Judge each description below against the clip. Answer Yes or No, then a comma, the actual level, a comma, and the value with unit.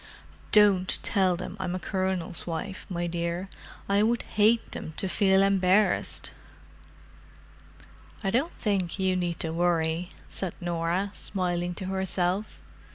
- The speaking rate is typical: No, slow, 125 wpm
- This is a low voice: No, medium, 185 Hz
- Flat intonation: Yes, narrow, 2.2 semitones